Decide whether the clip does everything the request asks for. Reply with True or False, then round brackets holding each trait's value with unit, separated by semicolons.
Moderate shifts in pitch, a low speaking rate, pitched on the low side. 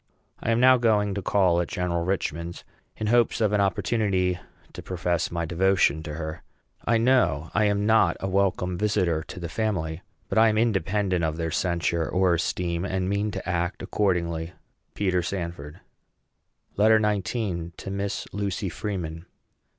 False (3.3 semitones; 160 wpm; 95 Hz)